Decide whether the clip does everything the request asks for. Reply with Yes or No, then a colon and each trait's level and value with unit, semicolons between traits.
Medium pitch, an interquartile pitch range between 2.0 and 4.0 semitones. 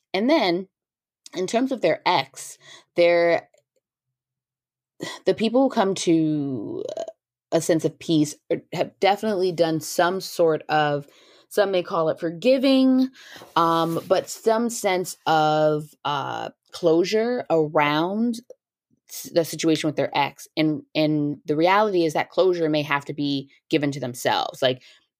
No: medium, 165 Hz; average, 4.8 semitones